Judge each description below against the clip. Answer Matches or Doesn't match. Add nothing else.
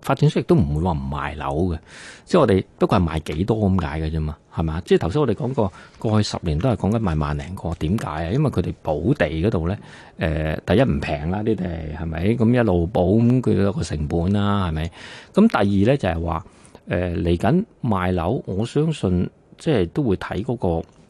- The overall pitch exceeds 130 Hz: Doesn't match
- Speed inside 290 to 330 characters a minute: Matches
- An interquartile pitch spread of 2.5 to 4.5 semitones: Doesn't match